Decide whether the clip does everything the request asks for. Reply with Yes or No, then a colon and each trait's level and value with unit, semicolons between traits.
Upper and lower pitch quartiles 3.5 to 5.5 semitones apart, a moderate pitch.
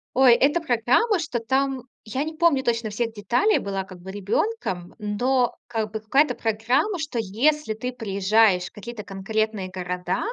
No: average, 4.7 semitones; high, 225 Hz